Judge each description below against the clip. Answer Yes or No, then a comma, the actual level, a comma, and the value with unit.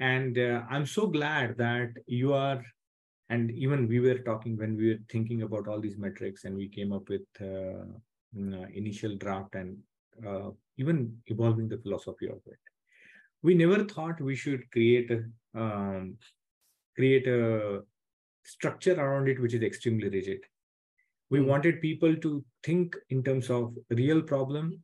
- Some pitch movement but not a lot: Yes, average, 4.6 semitones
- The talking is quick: No, average, 155 wpm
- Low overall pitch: Yes, low, 120 Hz